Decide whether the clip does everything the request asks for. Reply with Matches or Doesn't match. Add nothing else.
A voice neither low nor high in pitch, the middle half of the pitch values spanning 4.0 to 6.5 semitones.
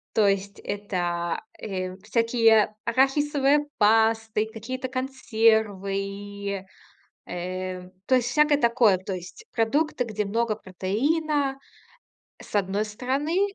Doesn't match